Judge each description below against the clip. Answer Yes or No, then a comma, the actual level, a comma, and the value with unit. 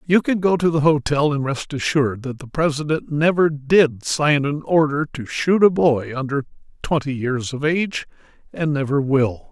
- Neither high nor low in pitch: Yes, medium, 145 Hz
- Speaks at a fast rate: No, average, 185 wpm